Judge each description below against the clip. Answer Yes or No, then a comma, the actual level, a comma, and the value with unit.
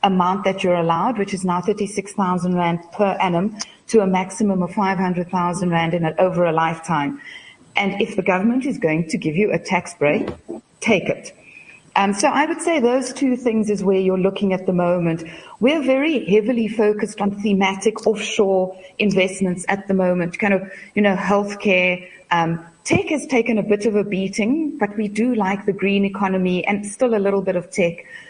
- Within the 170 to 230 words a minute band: Yes, fast, 205 wpm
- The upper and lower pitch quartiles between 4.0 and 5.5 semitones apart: No, average, 3.1 semitones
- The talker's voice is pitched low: No, high, 195 Hz